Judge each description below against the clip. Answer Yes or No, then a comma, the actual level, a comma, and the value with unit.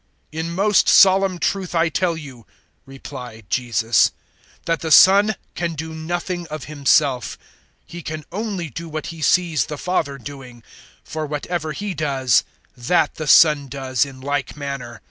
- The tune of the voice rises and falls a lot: No, average, 4.0 semitones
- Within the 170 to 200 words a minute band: No, average, 155 wpm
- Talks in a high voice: No, medium, 155 Hz